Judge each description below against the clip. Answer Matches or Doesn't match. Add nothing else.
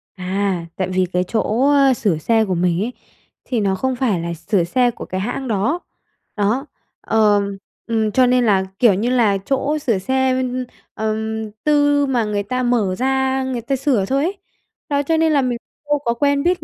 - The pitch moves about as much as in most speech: Matches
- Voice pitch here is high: Matches